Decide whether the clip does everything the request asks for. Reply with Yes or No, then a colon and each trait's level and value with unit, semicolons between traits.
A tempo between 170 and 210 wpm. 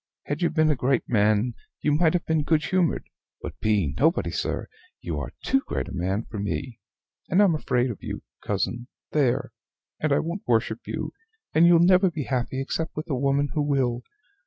Yes: average, 195 wpm